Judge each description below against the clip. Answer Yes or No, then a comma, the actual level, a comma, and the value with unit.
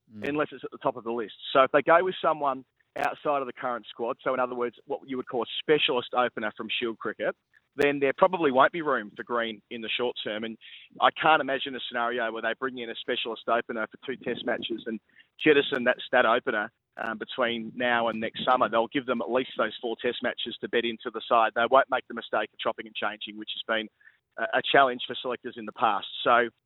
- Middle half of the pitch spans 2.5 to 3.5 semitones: Yes, average, 2.9 semitones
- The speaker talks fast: Yes, fast, 240 wpm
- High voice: No, low, 125 Hz